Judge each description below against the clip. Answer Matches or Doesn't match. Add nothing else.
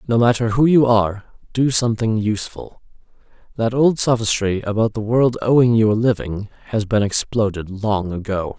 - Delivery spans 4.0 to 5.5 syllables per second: Matches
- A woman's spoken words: Doesn't match